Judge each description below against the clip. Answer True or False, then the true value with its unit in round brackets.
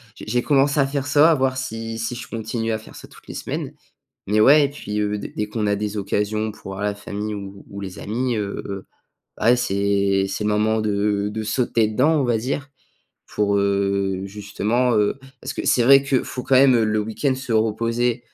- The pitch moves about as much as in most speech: True (3.4 semitones)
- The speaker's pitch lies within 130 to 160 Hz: False (110 Hz)